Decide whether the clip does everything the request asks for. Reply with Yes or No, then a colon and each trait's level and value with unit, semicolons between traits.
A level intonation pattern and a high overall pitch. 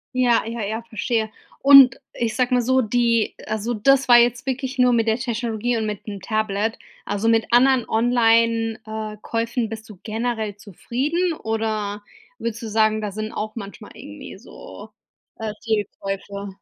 Yes: narrow, 2.1 semitones; high, 225 Hz